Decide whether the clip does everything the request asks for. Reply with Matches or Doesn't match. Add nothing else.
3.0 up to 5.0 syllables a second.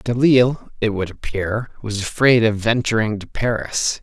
Matches